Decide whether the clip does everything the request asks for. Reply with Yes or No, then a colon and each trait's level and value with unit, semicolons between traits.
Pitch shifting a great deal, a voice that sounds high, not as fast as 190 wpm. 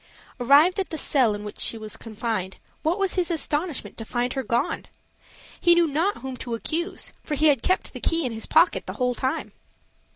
No: wide, 6.1 semitones; very high, 275 Hz; fast, 205 wpm